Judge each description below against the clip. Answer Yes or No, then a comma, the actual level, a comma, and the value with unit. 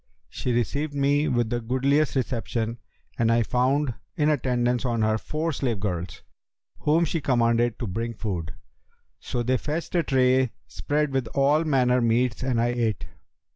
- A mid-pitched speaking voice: No, low, 125 Hz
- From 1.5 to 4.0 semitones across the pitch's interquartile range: Yes, average, 3.3 semitones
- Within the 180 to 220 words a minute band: No, average, 160 wpm